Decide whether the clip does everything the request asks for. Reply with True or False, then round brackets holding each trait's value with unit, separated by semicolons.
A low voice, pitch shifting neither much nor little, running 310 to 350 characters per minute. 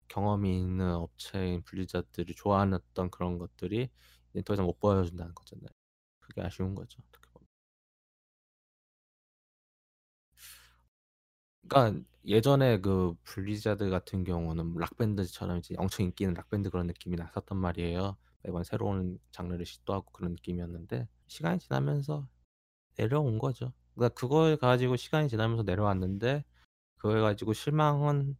True (95 Hz; 3.7 semitones; 325 characters per minute)